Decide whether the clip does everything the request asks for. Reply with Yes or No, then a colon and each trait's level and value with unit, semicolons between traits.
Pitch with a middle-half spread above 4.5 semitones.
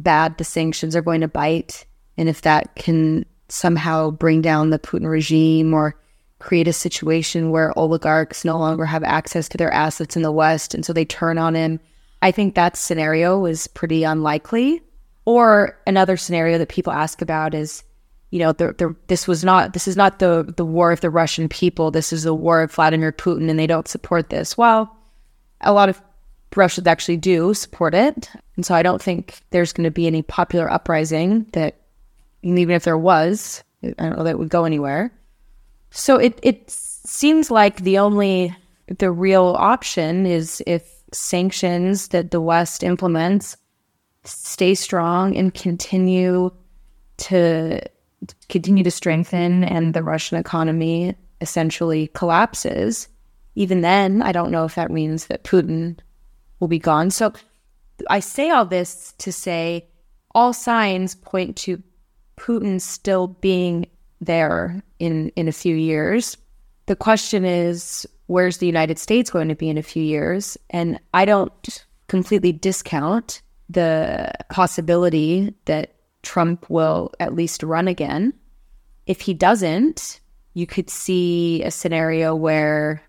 No: narrow, 2.6 semitones